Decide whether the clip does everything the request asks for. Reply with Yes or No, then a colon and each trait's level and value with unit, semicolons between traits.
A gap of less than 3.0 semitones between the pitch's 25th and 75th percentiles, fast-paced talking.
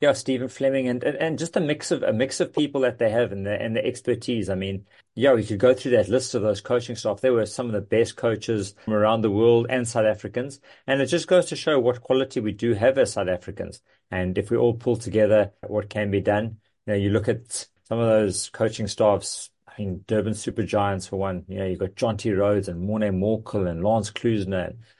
No: average, 3.3 semitones; fast, 250 wpm